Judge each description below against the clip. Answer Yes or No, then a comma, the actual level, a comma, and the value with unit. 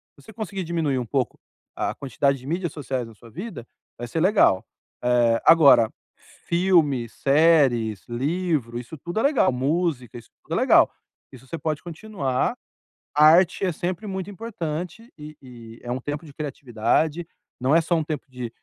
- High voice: No, medium, 150 Hz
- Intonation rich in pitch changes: Yes, wide, 5.7 semitones